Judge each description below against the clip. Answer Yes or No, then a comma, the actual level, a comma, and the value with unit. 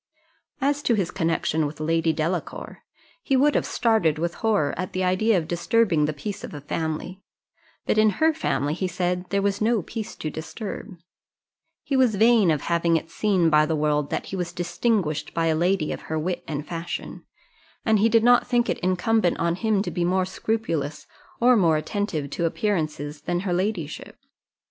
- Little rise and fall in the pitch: No, average, 5.2 semitones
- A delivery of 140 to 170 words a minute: No, average, 190 wpm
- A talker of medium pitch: Yes, medium, 180 Hz